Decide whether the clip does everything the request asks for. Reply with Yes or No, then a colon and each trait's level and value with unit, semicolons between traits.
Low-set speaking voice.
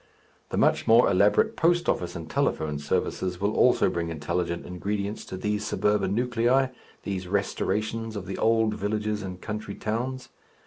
Yes: low, 105 Hz